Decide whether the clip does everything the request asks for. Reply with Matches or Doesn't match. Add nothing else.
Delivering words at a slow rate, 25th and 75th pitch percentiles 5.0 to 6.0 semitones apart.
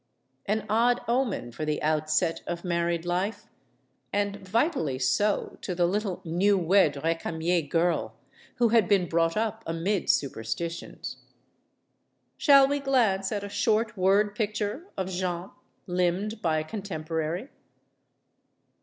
Doesn't match